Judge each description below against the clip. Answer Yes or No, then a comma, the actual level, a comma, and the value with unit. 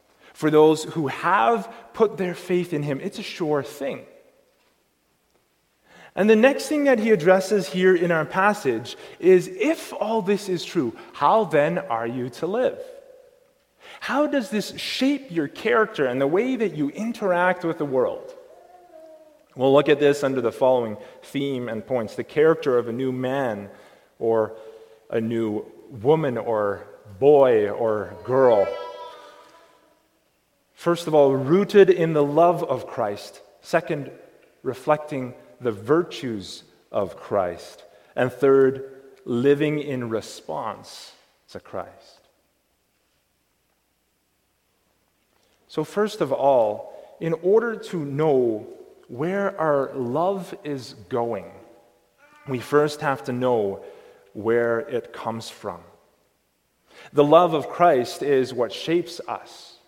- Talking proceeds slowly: Yes, slow, 125 wpm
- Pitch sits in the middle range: Yes, medium, 155 Hz